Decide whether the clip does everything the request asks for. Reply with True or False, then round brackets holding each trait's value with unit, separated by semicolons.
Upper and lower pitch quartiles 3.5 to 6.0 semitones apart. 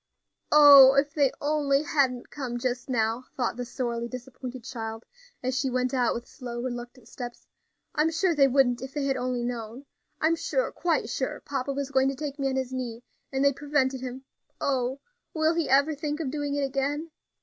False (2.5 semitones)